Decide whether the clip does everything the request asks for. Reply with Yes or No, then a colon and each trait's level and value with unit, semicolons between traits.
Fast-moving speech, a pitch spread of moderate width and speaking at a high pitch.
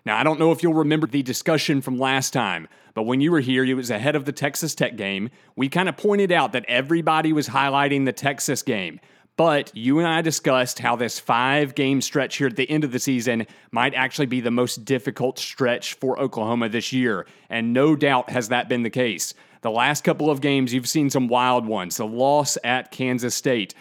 No: fast, 220 wpm; average, 3.2 semitones; low, 135 Hz